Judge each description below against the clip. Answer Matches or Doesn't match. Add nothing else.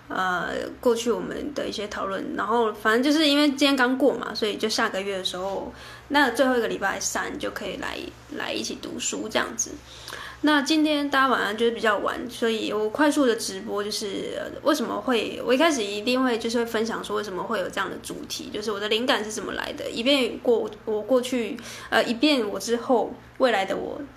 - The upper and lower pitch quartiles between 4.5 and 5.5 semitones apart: Doesn't match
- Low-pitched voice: Doesn't match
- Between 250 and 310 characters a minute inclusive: Doesn't match